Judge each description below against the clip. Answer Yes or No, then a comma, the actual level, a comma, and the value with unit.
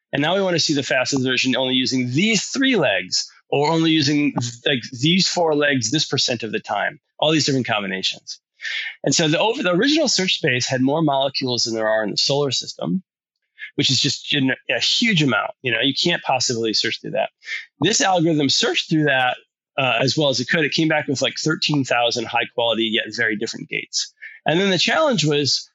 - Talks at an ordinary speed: No, fast, 210 wpm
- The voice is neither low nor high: Yes, medium, 145 Hz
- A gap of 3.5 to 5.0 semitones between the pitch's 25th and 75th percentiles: Yes, average, 4.2 semitones